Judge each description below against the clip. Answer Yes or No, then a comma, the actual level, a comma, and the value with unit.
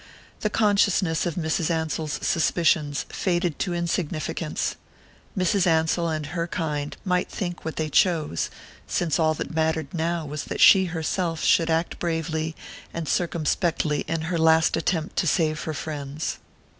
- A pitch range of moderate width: No, narrow, 1.8 semitones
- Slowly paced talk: No, average, 145 wpm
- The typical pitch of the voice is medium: Yes, medium, 160 Hz